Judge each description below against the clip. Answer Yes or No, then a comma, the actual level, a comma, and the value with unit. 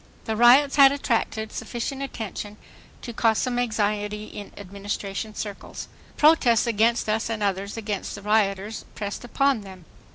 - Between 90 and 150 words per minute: Yes, average, 140 wpm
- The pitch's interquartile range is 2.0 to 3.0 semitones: Yes, average, 2.7 semitones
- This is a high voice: Yes, high, 220 Hz